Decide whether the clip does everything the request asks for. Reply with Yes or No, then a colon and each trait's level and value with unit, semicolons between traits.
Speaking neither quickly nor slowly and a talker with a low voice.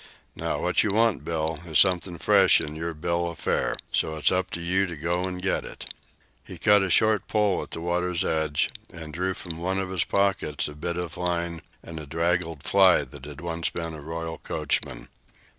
No: fast, 210 wpm; very low, 85 Hz